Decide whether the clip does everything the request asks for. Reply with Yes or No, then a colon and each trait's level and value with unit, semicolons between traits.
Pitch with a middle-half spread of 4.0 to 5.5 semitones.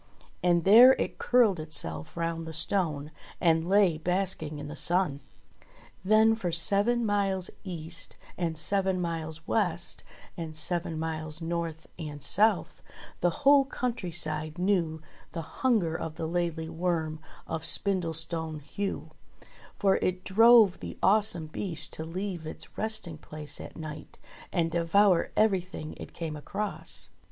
No: average, 3.5 semitones